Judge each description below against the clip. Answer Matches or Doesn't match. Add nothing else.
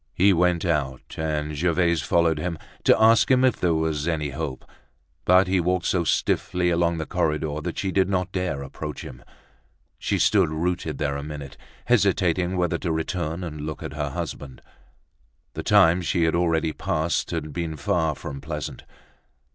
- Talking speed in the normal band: Matches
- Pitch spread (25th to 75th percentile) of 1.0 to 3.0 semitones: Matches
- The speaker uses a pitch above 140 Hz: Doesn't match